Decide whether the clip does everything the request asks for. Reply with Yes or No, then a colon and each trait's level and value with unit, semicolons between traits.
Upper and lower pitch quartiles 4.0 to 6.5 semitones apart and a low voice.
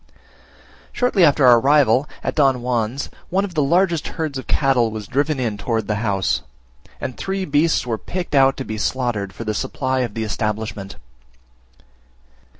Yes: average, 5.0 semitones; low, 130 Hz